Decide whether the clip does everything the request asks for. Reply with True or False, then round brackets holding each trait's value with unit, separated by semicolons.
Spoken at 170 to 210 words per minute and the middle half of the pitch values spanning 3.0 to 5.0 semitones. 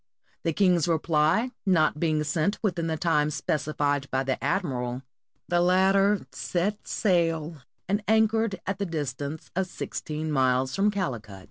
False (140 wpm; 4.7 semitones)